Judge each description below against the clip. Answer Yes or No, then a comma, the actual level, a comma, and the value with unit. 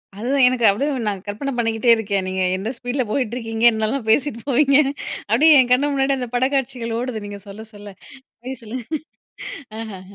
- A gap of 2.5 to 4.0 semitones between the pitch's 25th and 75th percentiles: Yes, average, 3.6 semitones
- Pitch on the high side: Yes, high, 235 Hz